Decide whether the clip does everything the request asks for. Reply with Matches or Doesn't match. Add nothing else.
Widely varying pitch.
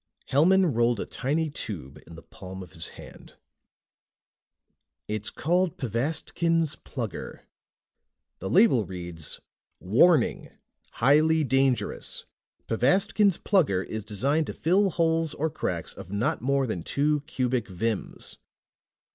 Matches